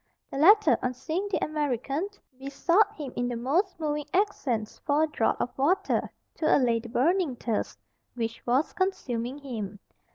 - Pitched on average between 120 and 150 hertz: No, very high, 280 Hz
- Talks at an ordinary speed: Yes, average, 160 wpm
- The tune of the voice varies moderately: No, wide, 5.8 semitones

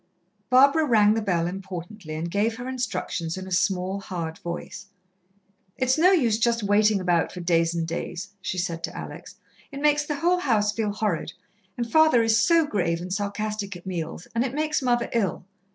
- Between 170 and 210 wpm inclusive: Yes, average, 185 wpm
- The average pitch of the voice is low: No, high, 205 Hz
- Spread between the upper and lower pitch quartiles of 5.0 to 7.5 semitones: Yes, wide, 5.6 semitones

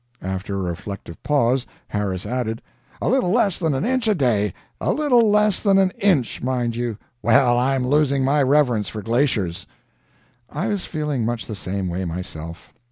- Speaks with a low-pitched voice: Yes, low, 125 Hz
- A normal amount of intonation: No, wide, 7.0 semitones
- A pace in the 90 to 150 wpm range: No, average, 170 wpm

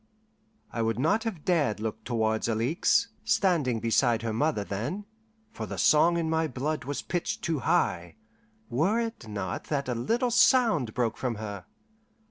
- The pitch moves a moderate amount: No, wide, 7.3 semitones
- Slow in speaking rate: No, average, 160 wpm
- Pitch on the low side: Yes, low, 130 Hz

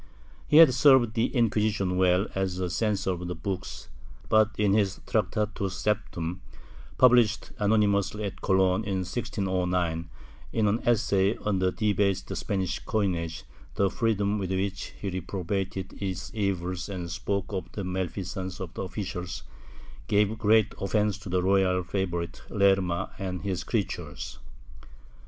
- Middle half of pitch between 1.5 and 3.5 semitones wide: Yes, narrow, 2.4 semitones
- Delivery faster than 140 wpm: No, slow, 135 wpm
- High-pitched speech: No, very low, 95 Hz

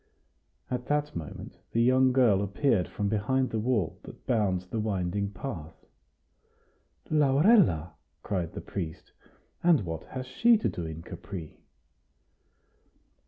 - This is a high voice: No, low, 105 Hz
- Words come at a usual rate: No, slow, 125 wpm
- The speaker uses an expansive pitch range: Yes, wide, 6.5 semitones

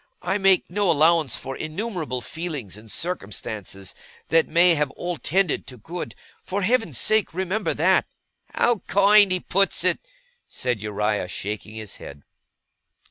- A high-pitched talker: No, medium, 165 Hz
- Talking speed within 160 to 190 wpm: No, average, 140 wpm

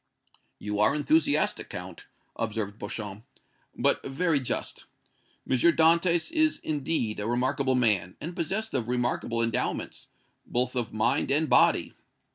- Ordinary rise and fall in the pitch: No, wide, 6.3 semitones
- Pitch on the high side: No, low, 130 Hz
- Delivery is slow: Yes, slow, 125 wpm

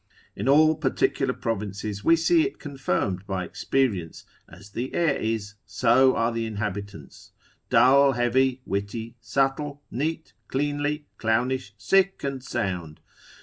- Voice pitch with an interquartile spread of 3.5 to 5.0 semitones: No, wide, 5.6 semitones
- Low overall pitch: Yes, low, 120 Hz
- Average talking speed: No, slow, 125 wpm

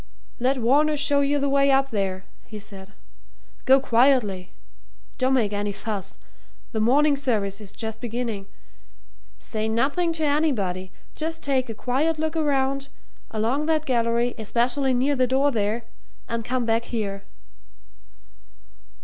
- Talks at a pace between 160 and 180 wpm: No, average, 140 wpm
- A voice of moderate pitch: No, very high, 250 Hz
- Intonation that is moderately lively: Yes, average, 4.4 semitones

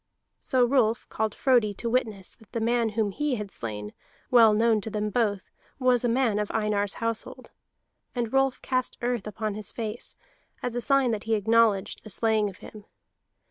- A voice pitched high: Yes, high, 225 Hz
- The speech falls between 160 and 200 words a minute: Yes, average, 180 wpm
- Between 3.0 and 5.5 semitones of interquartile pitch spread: No, narrow, 2.5 semitones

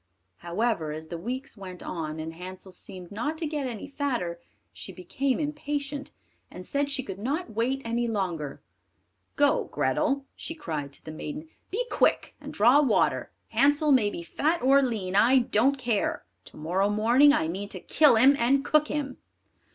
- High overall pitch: Yes, high, 240 Hz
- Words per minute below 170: No, average, 175 wpm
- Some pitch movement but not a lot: No, wide, 7.3 semitones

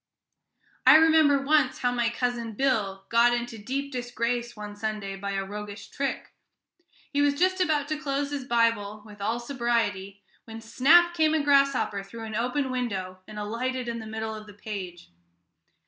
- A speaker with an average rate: Yes, average, 170 wpm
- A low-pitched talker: No, high, 235 Hz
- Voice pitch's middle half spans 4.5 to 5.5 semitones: Yes, average, 4.8 semitones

